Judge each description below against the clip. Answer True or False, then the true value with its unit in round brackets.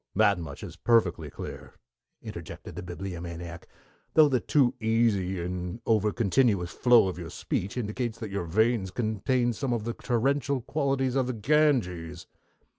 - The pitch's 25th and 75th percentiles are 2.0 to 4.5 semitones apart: False (5.4 semitones)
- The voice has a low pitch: True (110 Hz)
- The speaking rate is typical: True (145 wpm)